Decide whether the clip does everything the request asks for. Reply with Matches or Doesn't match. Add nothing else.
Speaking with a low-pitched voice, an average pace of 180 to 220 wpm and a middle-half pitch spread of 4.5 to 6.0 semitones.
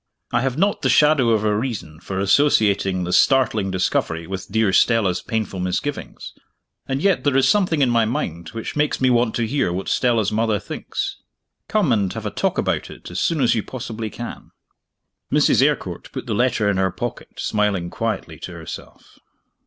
Matches